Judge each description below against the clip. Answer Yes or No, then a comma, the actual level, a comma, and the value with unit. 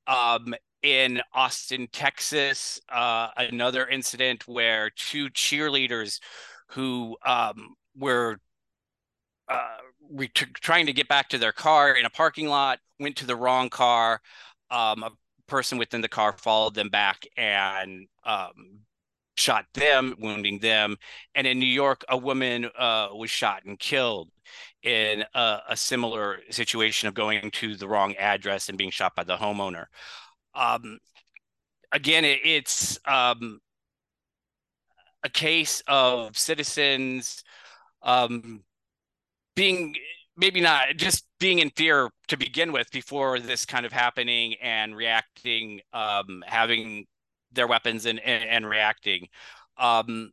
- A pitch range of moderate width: Yes, average, 3.7 semitones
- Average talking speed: No, slow, 130 wpm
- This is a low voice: Yes, low, 120 Hz